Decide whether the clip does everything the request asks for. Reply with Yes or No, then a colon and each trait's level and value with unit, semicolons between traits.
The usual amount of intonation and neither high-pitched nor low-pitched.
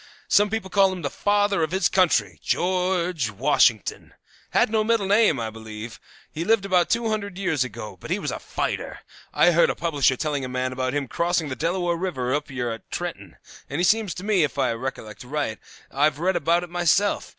No: wide, 6.6 semitones; medium, 165 Hz